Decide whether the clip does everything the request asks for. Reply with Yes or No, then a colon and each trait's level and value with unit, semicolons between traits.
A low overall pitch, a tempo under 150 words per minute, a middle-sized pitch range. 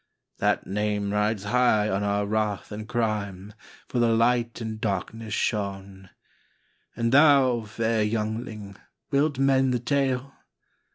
Yes: low, 110 Hz; slow, 135 wpm; average, 3.0 semitones